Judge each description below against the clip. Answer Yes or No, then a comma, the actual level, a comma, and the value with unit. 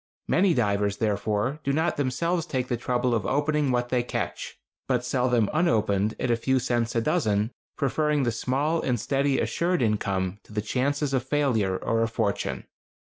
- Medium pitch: No, low, 125 Hz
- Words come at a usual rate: Yes, average, 175 wpm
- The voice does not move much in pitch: No, average, 4.4 semitones